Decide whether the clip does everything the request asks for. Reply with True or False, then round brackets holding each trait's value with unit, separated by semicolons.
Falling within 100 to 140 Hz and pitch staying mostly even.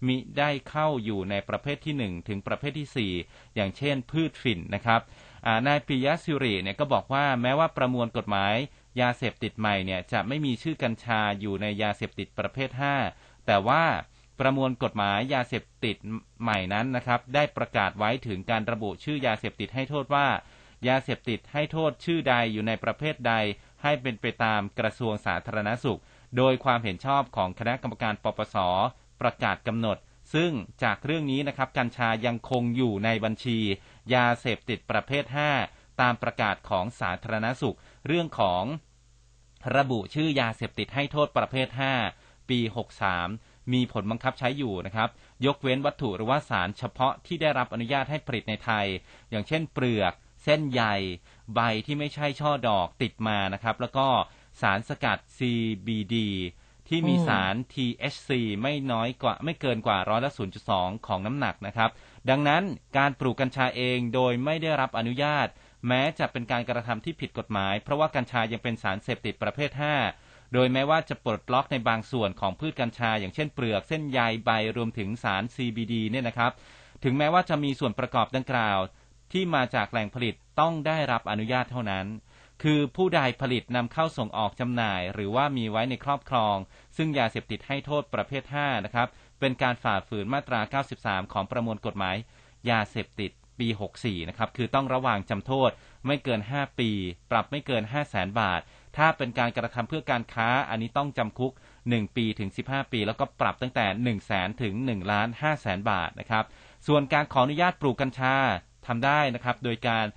False (120 Hz; 3.8 semitones)